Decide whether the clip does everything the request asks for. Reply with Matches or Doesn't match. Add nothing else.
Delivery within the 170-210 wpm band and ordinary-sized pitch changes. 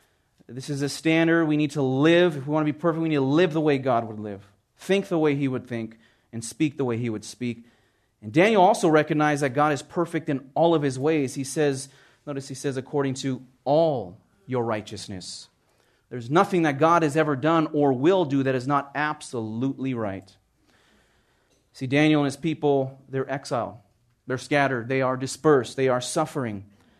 Matches